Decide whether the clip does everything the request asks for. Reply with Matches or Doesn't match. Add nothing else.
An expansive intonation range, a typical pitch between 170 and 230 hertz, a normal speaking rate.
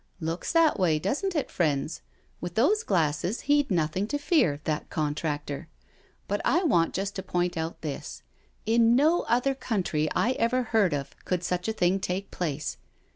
Matches